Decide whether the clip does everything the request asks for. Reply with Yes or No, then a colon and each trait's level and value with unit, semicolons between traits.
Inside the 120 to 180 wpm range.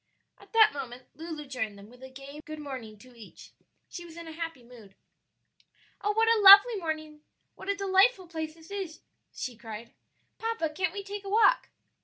No: average, 190 wpm